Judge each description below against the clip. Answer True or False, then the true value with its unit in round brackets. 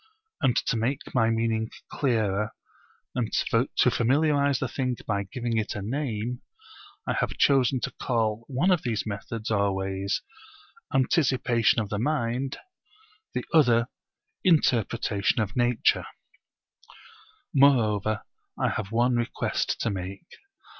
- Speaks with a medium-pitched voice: False (115 Hz)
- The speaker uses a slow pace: True (125 wpm)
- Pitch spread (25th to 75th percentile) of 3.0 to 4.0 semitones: True (3.4 semitones)